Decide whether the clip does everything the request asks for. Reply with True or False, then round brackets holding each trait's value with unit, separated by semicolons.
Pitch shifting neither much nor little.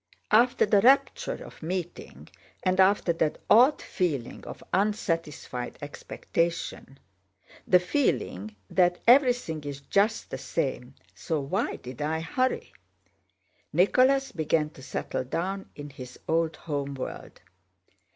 False (6.1 semitones)